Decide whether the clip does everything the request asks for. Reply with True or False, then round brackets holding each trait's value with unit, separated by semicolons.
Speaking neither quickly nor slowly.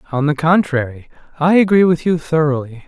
True (165 wpm)